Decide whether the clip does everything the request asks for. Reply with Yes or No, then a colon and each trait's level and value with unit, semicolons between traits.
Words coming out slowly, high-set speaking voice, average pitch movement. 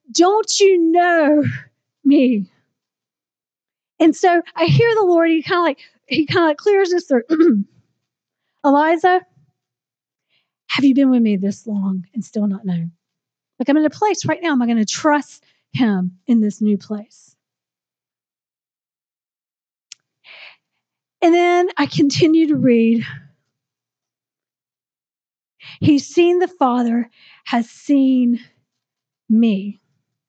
No: slow, 125 wpm; very high, 260 Hz; wide, 8.2 semitones